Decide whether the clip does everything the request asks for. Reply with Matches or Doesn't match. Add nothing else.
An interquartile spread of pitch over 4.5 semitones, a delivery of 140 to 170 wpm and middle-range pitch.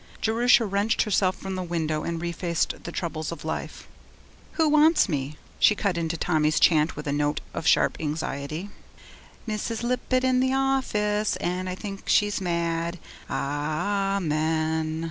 Matches